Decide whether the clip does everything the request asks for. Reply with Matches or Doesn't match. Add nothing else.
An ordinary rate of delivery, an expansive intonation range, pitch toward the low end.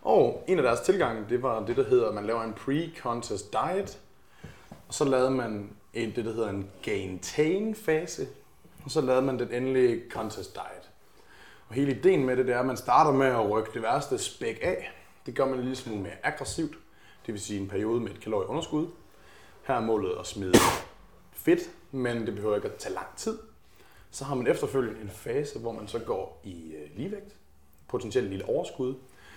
Matches